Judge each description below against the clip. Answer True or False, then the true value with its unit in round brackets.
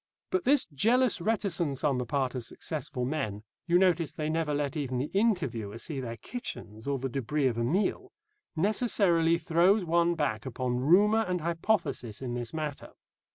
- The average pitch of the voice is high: False (155 Hz)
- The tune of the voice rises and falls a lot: True (6.1 semitones)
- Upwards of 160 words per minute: True (170 wpm)